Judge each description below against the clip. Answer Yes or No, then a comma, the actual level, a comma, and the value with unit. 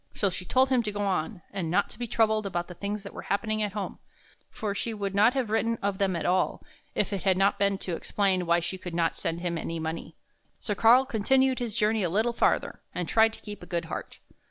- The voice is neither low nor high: No, high, 200 Hz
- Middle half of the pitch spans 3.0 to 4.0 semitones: Yes, average, 3.5 semitones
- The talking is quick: Yes, fast, 250 wpm